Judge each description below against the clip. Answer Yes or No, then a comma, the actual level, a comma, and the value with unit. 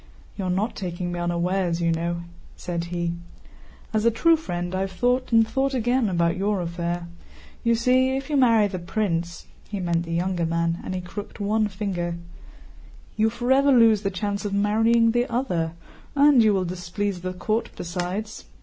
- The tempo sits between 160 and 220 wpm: Yes, average, 175 wpm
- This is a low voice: No, high, 195 Hz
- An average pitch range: Yes, average, 4.7 semitones